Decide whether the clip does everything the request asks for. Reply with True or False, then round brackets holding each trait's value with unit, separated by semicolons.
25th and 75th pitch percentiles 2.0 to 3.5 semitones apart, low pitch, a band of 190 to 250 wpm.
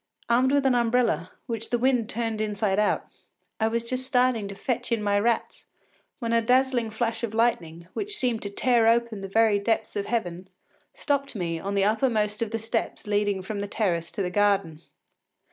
False (2.9 semitones; 225 Hz; 195 wpm)